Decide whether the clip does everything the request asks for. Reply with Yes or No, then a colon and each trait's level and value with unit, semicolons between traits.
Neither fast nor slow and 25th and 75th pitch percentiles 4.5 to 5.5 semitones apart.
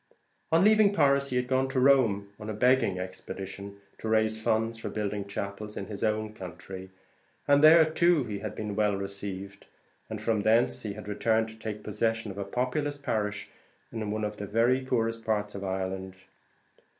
No: average, 185 wpm; average, 3.7 semitones